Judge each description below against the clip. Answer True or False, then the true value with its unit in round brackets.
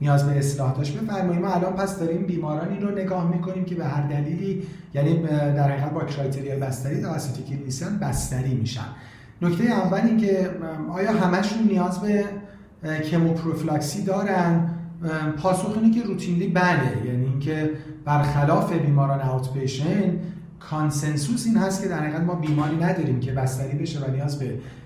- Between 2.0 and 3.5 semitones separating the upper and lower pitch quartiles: False (4.5 semitones)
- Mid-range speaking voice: True (160 Hz)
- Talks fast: False (145 wpm)